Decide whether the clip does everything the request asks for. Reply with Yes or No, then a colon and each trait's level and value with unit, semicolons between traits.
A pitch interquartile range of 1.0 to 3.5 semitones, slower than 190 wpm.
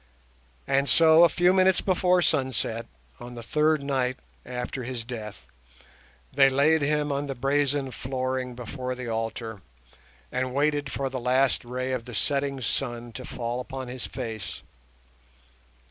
Yes: narrow, 2.6 semitones; average, 145 wpm